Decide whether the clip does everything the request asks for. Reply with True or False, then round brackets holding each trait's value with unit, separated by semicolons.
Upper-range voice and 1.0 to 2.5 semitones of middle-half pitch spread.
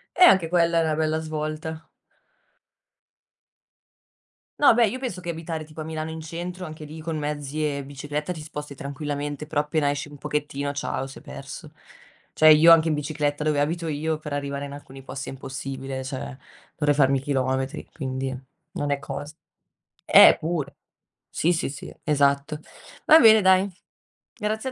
False (150 Hz; 2.2 semitones)